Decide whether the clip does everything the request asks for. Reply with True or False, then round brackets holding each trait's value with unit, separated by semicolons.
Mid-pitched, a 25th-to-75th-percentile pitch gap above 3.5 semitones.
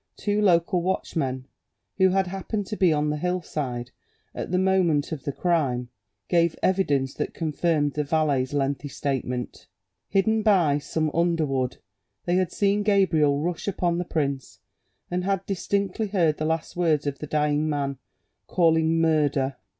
True (160 Hz; 4.2 semitones)